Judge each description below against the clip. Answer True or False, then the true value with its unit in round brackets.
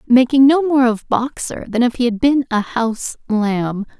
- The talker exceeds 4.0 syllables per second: True (4.6 syllables/s)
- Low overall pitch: False (245 Hz)